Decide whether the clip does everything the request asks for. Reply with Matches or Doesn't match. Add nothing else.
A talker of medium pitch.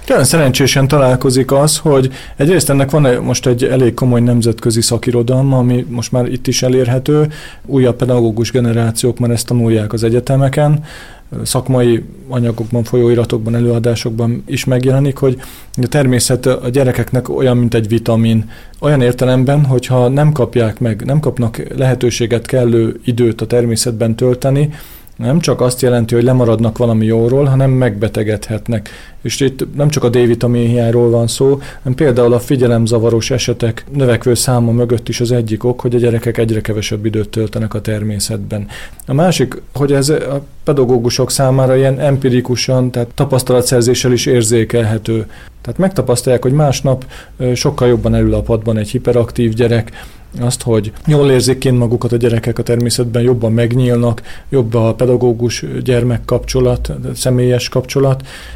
Doesn't match